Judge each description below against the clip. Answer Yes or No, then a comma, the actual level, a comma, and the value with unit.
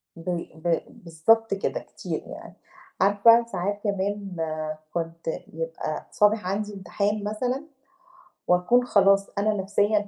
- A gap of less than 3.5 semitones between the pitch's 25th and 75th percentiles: Yes, average, 2.9 semitones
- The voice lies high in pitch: Yes, high, 200 Hz